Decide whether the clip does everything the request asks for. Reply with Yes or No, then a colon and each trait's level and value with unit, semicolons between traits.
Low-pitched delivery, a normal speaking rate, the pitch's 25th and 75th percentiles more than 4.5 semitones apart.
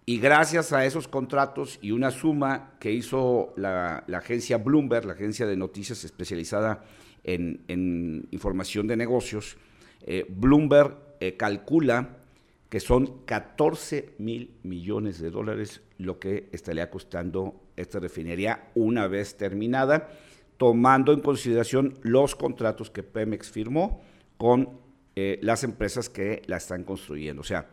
Yes: low, 110 Hz; average, 135 wpm; wide, 5.4 semitones